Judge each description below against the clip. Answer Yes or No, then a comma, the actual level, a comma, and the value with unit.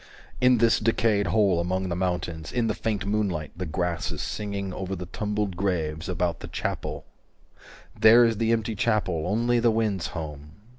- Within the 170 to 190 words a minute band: Yes, average, 180 wpm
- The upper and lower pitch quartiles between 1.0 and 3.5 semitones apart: No, average, 4.0 semitones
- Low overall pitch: Yes, low, 100 Hz